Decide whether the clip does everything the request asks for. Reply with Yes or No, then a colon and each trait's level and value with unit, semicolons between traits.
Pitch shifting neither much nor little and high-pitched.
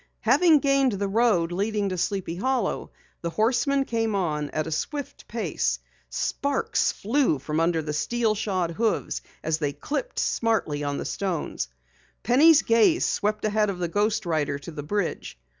No: wide, 6.2 semitones; high, 205 Hz